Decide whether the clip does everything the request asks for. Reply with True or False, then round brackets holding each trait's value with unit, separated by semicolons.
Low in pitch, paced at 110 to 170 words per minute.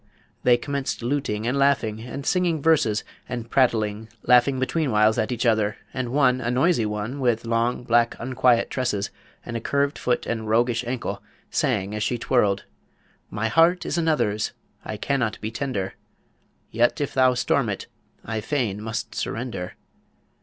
True (120 Hz; 155 wpm)